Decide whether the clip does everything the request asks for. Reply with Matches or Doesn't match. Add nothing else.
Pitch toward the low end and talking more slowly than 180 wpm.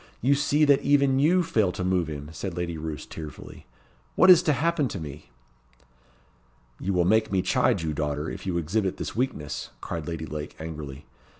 Doesn't match